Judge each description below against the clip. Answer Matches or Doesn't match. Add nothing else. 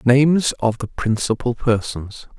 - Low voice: Matches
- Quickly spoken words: Doesn't match